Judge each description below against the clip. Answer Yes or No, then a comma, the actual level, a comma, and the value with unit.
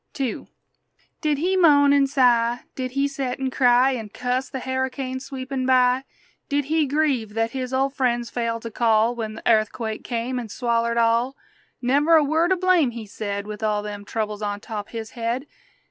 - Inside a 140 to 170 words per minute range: No, average, 185 wpm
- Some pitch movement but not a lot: Yes, average, 3.1 semitones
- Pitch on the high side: Yes, very high, 250 Hz